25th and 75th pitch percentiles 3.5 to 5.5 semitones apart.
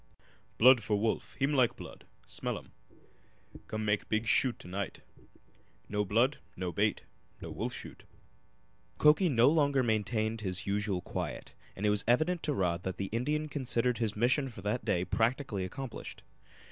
Yes: average, 4.4 semitones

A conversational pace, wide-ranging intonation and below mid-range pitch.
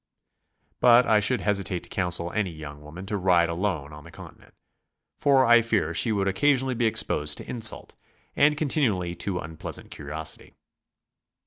Yes: average, 170 wpm; wide, 6.1 semitones; very low, 95 Hz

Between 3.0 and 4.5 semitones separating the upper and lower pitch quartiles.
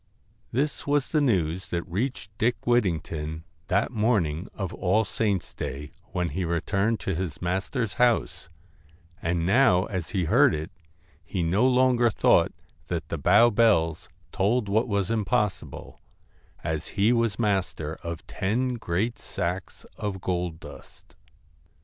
No: average, 5.1 semitones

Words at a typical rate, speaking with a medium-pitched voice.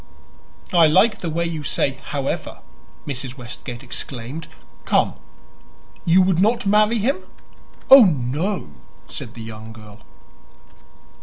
No: slow, 120 wpm; medium, 155 Hz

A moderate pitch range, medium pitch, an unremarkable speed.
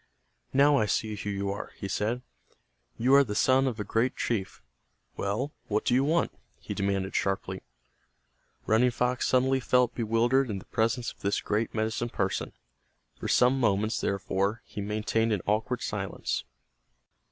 No: average, 3.7 semitones; low, 110 Hz; average, 160 wpm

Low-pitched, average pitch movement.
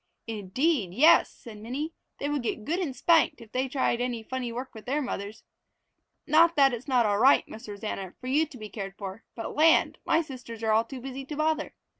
No: very high, 250 Hz; average, 4.9 semitones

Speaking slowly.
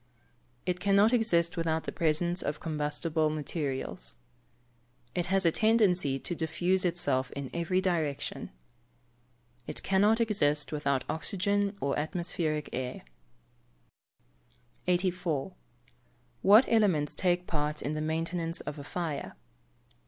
Yes: slow, 115 wpm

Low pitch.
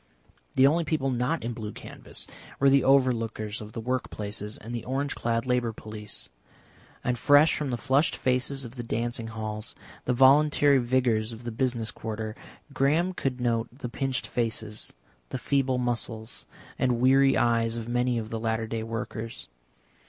Yes: low, 120 Hz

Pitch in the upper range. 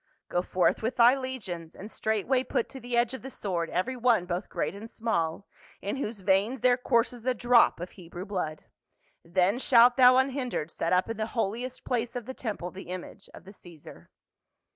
Yes: high, 225 Hz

